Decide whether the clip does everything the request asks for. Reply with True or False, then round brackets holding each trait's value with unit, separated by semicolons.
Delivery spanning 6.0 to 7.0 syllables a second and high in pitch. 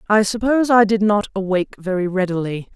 True (6.1 syllables/s; 200 Hz)